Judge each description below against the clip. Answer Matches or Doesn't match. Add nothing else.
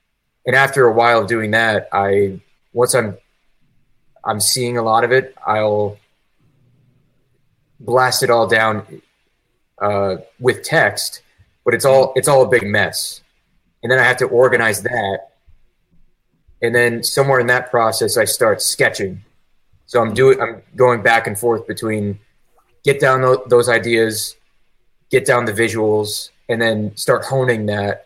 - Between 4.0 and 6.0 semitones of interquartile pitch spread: Doesn't match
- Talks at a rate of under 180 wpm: Matches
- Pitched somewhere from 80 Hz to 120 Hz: Matches